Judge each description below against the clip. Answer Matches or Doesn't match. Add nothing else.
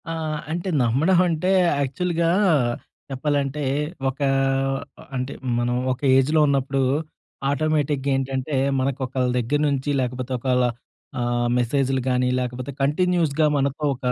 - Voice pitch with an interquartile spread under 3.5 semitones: Matches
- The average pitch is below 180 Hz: Matches